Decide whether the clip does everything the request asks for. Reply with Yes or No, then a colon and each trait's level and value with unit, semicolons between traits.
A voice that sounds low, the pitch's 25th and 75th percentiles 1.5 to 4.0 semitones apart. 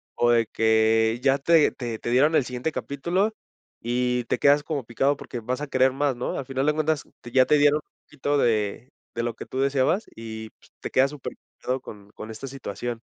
Yes: low, 130 Hz; average, 3.5 semitones